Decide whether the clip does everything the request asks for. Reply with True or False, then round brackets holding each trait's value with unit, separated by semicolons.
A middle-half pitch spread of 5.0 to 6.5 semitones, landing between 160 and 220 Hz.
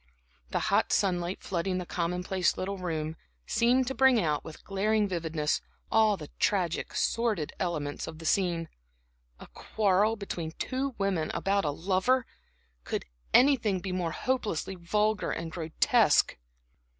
False (4.3 semitones; 185 Hz)